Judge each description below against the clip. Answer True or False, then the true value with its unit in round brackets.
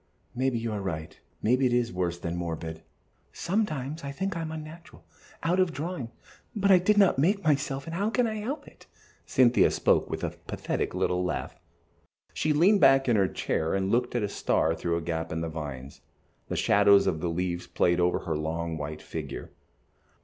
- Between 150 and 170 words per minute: False (200 wpm)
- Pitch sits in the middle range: False (120 Hz)